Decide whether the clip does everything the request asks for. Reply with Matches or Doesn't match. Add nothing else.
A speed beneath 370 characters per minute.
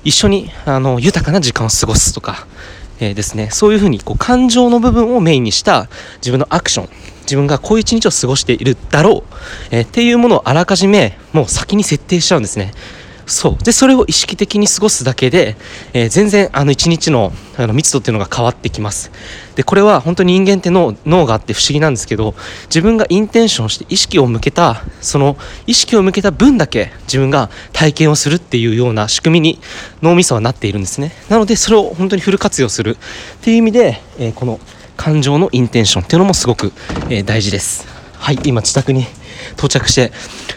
Doesn't match